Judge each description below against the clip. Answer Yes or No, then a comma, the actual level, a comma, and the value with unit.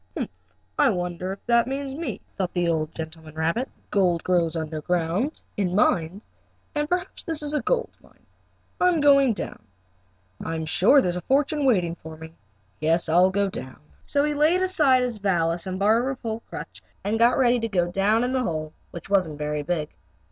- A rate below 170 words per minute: No, average, 195 wpm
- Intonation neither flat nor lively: No, wide, 7.9 semitones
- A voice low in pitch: No, high, 195 Hz